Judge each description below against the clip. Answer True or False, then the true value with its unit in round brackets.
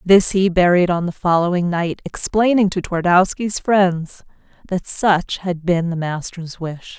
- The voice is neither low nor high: True (180 Hz)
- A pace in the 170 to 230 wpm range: False (155 wpm)